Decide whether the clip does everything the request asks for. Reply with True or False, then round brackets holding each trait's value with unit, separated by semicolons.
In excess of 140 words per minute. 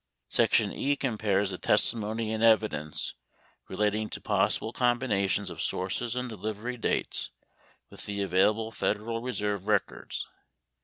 False (135 wpm)